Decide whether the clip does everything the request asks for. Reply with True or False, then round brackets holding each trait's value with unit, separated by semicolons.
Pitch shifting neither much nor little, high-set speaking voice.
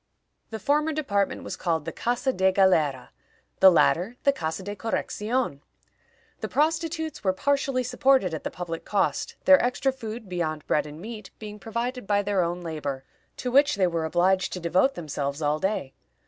False (6.9 semitones; 195 Hz)